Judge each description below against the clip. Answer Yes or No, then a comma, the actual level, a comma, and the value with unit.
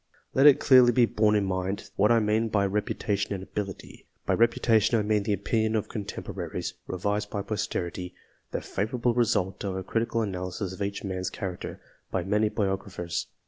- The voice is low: Yes, low, 105 Hz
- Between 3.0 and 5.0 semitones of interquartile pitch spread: No, narrow, 2.6 semitones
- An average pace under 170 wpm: No, average, 180 wpm